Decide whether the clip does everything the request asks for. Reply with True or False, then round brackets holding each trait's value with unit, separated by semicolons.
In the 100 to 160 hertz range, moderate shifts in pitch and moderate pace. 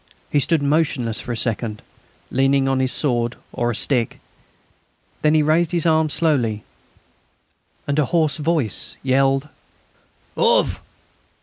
False (140 Hz; 4.3 semitones; 130 wpm)